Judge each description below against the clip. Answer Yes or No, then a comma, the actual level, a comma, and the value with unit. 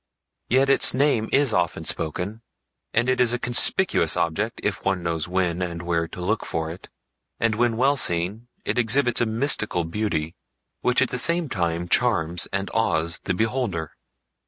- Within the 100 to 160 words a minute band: No, average, 170 wpm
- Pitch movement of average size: No, wide, 6.1 semitones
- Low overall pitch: Yes, low, 105 Hz